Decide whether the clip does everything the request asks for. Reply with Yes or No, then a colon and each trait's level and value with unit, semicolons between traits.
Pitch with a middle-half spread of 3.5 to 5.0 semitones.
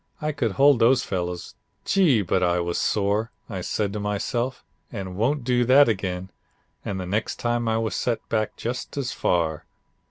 Yes: average, 4.6 semitones